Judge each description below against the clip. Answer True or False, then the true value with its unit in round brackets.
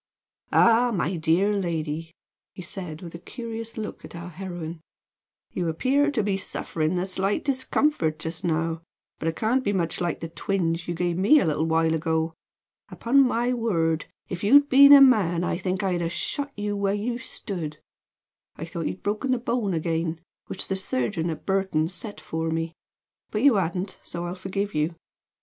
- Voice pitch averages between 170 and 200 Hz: True (185 Hz)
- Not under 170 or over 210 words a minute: True (185 wpm)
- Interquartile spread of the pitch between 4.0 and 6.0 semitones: True (4.9 semitones)